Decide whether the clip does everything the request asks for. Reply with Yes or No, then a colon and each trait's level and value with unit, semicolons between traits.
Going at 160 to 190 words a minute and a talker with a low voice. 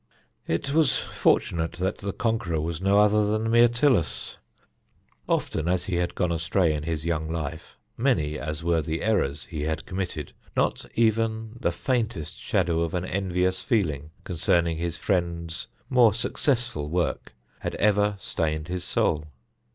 No: average, 150 wpm; very low, 90 Hz